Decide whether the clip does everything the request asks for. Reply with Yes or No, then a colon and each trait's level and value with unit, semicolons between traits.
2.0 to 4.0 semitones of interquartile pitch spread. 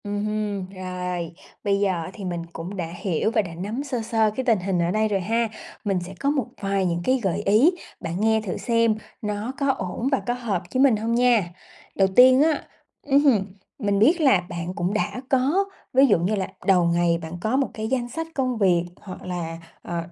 No: average, 5.0 semitones